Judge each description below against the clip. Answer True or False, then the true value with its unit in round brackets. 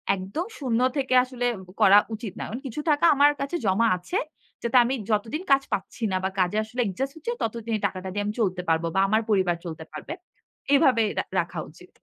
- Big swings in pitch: True (5.7 semitones)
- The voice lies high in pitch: True (225 Hz)